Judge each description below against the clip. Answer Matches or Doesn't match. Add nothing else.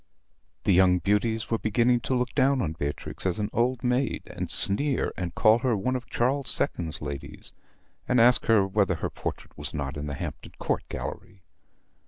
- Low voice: Matches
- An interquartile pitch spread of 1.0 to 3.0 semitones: Doesn't match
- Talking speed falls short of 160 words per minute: Doesn't match